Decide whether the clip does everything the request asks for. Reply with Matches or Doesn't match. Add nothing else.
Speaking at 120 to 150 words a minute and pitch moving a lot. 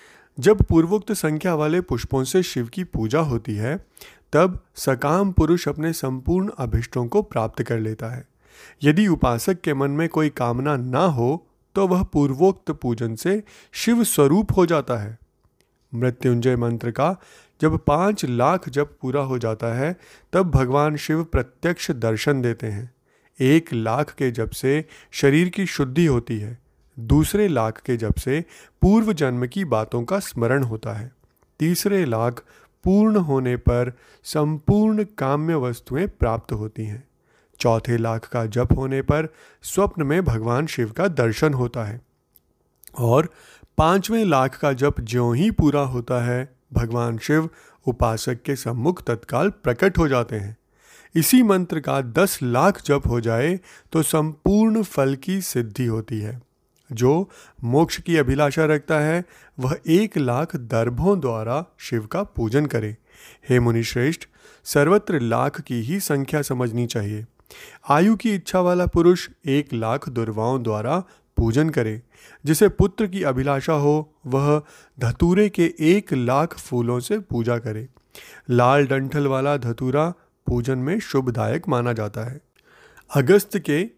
Matches